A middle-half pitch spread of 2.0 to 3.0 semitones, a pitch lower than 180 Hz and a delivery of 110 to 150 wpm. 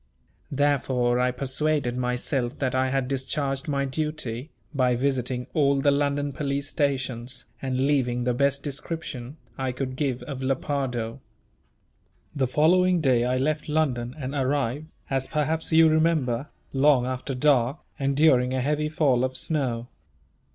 Yes: narrow, 2.5 semitones; low, 135 Hz; average, 145 wpm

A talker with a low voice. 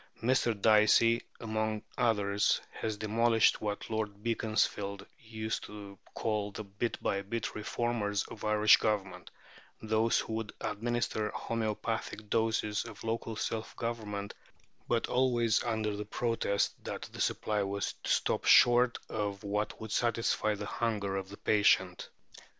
Yes: low, 110 Hz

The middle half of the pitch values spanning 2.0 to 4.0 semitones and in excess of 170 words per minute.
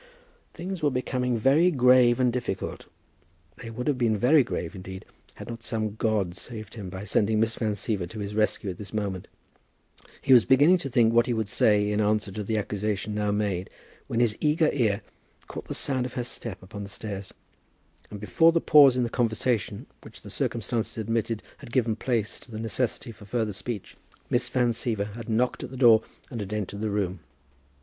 Yes: average, 3.2 semitones; average, 200 wpm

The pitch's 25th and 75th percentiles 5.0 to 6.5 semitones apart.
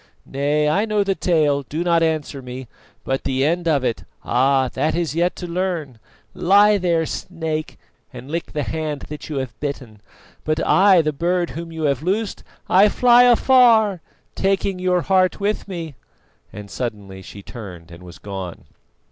Yes: wide, 5.5 semitones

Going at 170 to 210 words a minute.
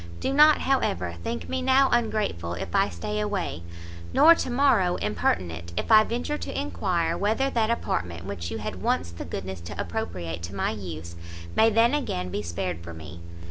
Yes: average, 180 wpm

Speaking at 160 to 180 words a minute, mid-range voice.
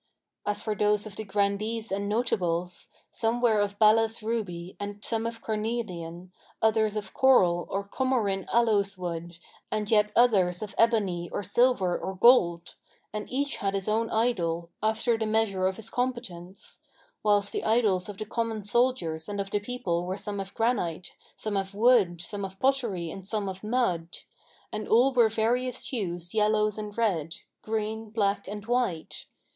No: average, 170 wpm; high, 210 Hz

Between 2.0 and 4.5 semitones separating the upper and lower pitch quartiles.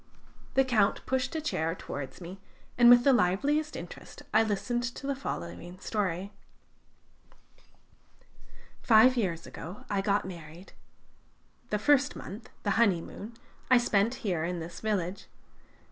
No: average, 5.3 semitones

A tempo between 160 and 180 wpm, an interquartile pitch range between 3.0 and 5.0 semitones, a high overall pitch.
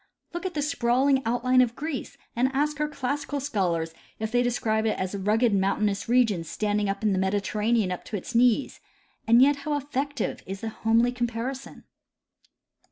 Yes: average, 175 wpm; average, 4.5 semitones; high, 235 Hz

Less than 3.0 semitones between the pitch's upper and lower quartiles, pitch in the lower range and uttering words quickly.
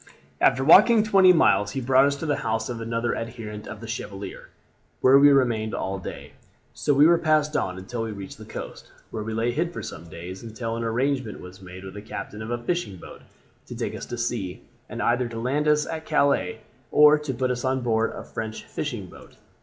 No: average, 4.6 semitones; low, 120 Hz; fast, 220 wpm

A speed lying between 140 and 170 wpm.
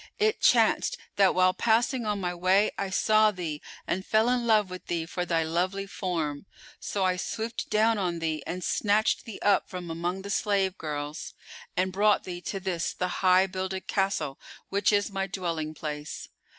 No: average, 180 wpm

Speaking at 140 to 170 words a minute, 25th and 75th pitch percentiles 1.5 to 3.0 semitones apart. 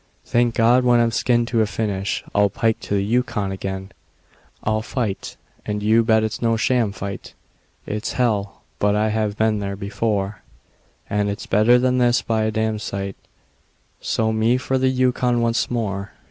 Yes: average, 165 wpm; narrow, 2.6 semitones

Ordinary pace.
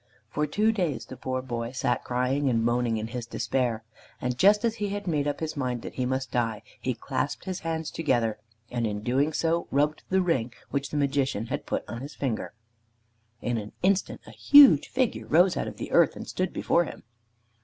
No: fast, 210 wpm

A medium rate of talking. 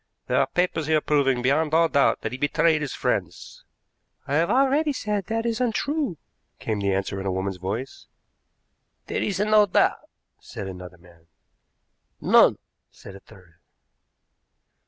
Yes: average, 155 wpm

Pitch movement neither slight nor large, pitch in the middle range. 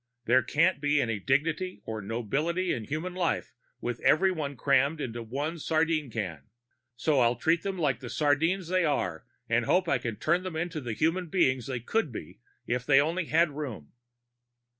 No: wide, 5.7 semitones; medium, 145 Hz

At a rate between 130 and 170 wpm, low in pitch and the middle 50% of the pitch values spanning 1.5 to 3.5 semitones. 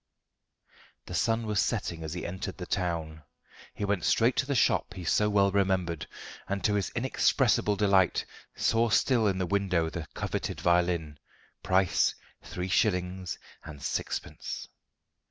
Yes: average, 145 wpm; very low, 95 Hz; average, 2.9 semitones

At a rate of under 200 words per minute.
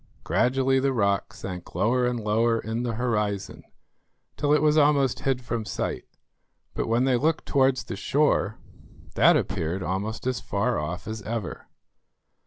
Yes: average, 155 wpm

